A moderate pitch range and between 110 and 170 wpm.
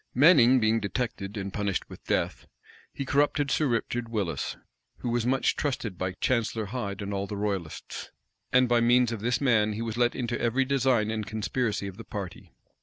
No: average, 3.4 semitones; average, 185 wpm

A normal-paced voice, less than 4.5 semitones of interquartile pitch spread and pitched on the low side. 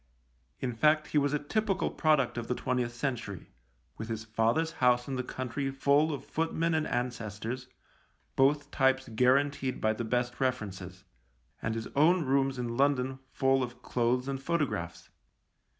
Yes: average, 165 wpm; average, 3.4 semitones; low, 130 Hz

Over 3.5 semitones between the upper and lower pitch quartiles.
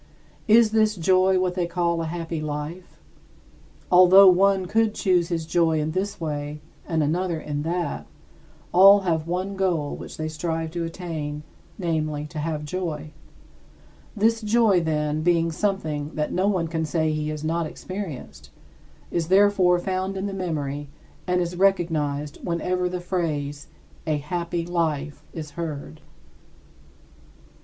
No: average, 3.2 semitones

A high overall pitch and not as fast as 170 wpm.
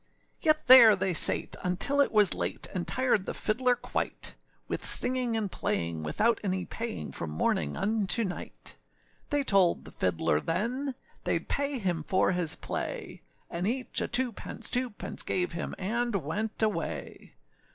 Yes: high, 205 Hz; average, 160 wpm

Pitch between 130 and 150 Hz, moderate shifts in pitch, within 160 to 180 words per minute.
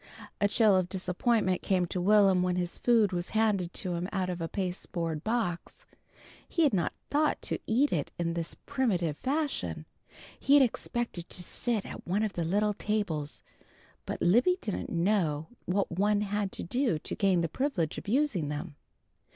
No: high, 190 Hz; average, 4.1 semitones; average, 175 wpm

